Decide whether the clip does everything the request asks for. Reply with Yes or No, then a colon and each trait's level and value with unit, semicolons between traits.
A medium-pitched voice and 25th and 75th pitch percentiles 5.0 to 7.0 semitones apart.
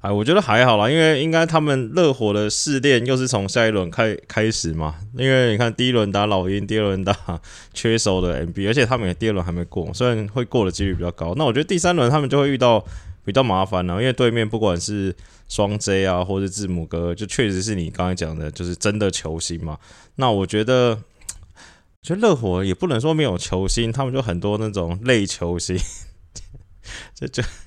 No: low, 105 Hz; average, 5.3 semitones